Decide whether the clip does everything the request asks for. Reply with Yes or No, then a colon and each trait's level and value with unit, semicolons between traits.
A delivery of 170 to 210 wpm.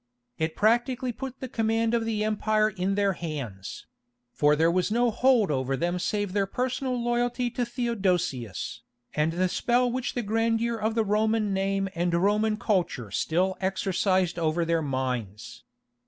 No: average, 155 wpm